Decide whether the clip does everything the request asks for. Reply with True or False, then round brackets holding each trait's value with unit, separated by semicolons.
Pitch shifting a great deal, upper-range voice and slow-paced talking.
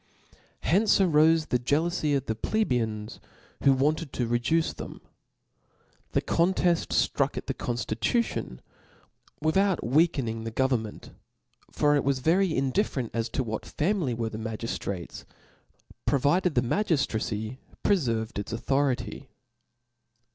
False (6.2 semitones; 135 Hz; 120 wpm)